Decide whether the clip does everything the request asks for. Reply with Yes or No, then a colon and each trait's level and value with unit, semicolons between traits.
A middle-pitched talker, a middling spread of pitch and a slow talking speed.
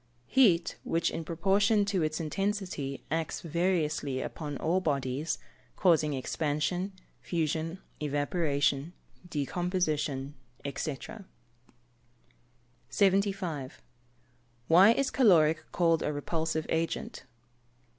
Yes: medium, 160 Hz; average, 3.8 semitones; slow, 90 wpm